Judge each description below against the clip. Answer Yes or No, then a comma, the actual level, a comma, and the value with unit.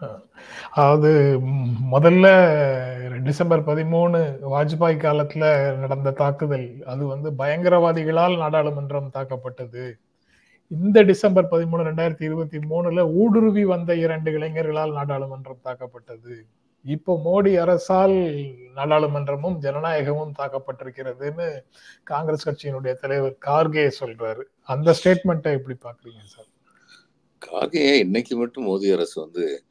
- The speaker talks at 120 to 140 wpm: No, average, 85 wpm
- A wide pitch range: No, average, 3.8 semitones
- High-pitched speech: No, medium, 150 Hz